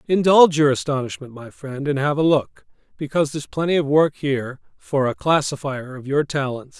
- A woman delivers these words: No, male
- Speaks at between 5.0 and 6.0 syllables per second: Yes, 5.6 syllables/s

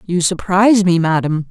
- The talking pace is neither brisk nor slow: Yes, average, 160 wpm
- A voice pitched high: No, medium, 180 Hz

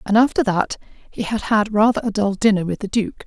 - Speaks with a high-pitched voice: Yes, high, 210 Hz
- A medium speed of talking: No, fast, 240 wpm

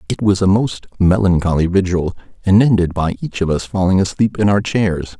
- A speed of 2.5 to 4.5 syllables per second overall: No, 5.2 syllables/s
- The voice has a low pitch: Yes, very low, 95 Hz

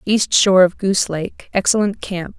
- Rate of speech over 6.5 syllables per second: No, 5.0 syllables/s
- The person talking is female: Yes, female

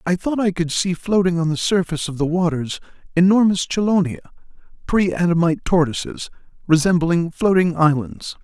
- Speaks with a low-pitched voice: No, medium, 175 Hz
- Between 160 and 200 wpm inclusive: No, average, 140 wpm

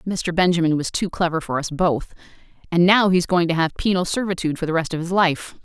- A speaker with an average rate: No, fast, 245 wpm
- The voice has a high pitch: No, medium, 170 Hz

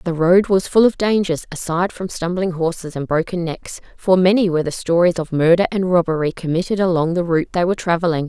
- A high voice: No, medium, 175 Hz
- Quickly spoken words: Yes, fast, 210 wpm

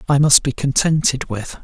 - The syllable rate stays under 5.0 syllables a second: Yes, 4.8 syllables/s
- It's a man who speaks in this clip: Yes, male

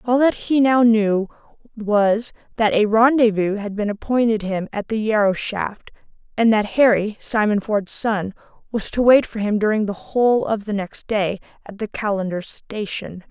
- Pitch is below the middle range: No, high, 210 Hz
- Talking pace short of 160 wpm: No, average, 175 wpm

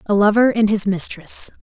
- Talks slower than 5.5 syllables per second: Yes, 5.0 syllables/s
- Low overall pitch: No, high, 205 Hz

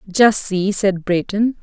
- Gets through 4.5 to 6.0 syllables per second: No, 3.9 syllables/s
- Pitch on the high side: Yes, high, 200 Hz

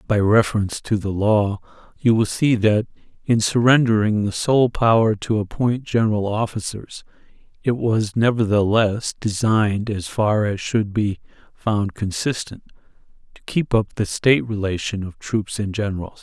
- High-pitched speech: No, low, 110 Hz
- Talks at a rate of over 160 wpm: No, average, 145 wpm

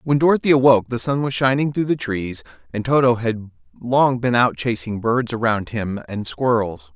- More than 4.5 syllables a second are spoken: Yes, 5.0 syllables/s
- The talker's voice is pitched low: Yes, low, 120 Hz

